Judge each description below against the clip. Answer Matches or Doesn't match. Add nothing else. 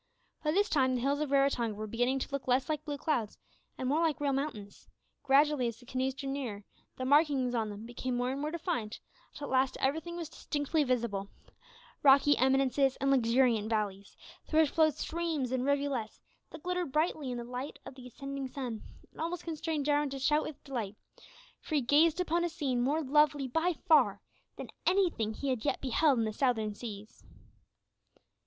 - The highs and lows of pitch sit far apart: Doesn't match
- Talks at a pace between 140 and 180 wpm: Doesn't match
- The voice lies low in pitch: Doesn't match